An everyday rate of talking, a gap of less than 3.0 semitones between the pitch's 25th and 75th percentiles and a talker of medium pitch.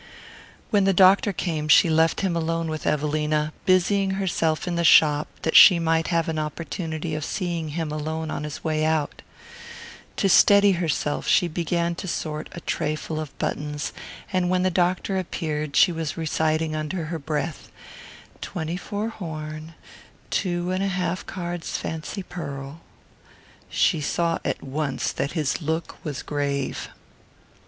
Yes: average, 150 wpm; narrow, 2.5 semitones; medium, 160 Hz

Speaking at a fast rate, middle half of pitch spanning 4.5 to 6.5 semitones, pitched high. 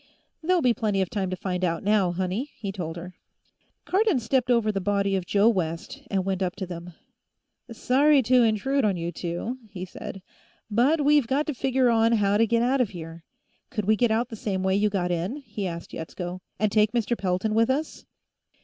Yes: fast, 210 wpm; average, 4.9 semitones; high, 210 Hz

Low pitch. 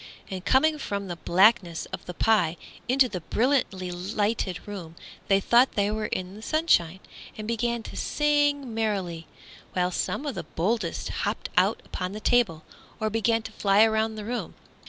No: high, 215 Hz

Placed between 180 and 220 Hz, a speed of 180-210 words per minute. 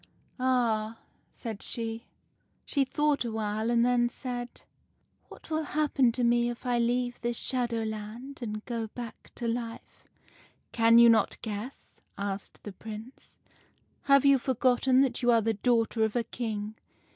No: high, 235 Hz; average, 185 wpm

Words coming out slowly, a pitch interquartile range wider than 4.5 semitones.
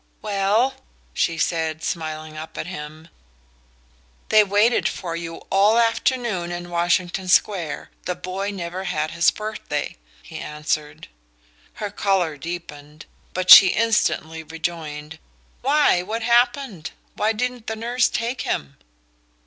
Yes: slow, 125 wpm; average, 5.0 semitones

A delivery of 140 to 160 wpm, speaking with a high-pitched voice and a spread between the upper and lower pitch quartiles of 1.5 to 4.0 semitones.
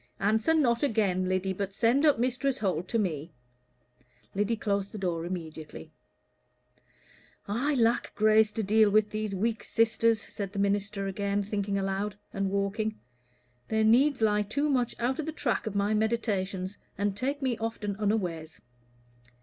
Yes: average, 155 wpm; high, 210 Hz; average, 2.7 semitones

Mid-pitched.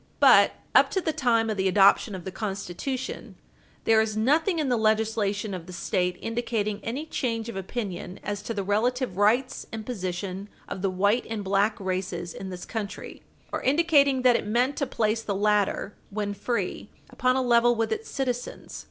No: high, 220 Hz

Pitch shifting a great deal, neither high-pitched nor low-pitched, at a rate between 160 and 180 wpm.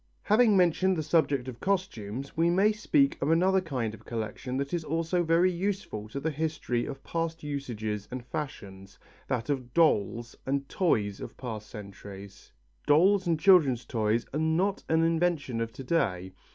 Yes: wide, 6.9 semitones; medium, 145 Hz; average, 165 wpm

